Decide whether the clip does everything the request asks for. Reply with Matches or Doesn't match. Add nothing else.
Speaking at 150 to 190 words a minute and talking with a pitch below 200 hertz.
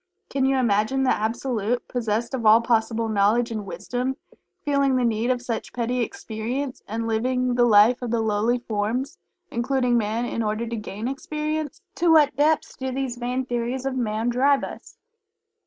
Doesn't match